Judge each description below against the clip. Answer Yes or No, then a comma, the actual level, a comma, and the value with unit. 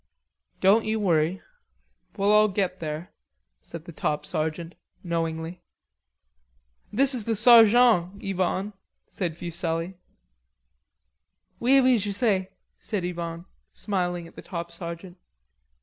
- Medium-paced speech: No, slow, 115 wpm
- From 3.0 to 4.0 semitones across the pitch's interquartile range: Yes, average, 3.7 semitones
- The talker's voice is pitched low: No, medium, 180 Hz